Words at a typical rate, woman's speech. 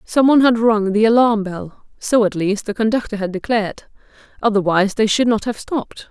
Yes: average, 185 wpm; female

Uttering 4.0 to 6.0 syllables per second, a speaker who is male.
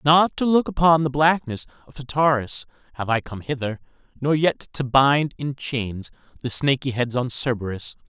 Yes: 4.8 syllables/s; male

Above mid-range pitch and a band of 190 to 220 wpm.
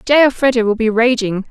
Yes: high, 235 Hz; average, 200 wpm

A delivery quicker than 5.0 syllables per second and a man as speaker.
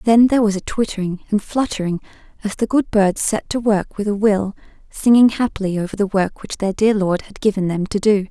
No: 5.5 syllables/s; female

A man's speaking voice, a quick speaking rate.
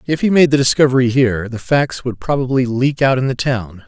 Yes: male; fast, 230 wpm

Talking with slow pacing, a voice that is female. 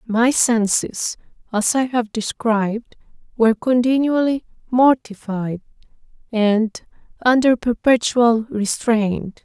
Yes: slow, 85 wpm; female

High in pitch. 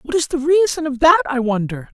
Yes: very high, 255 Hz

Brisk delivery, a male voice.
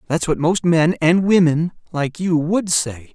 No: average, 155 wpm; male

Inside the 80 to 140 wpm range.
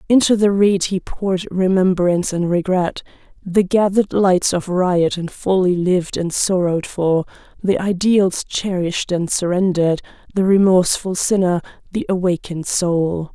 Yes: slow, 135 wpm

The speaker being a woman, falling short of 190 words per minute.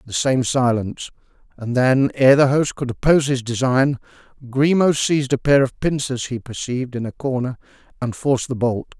No: male; average, 180 wpm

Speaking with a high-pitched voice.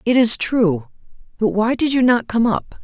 Yes: high, 240 Hz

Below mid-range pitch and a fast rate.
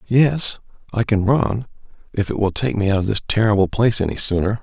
Yes: low, 105 Hz; fast, 210 wpm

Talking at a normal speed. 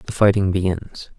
Yes: average, 150 wpm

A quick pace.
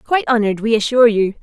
Yes: fast, 210 wpm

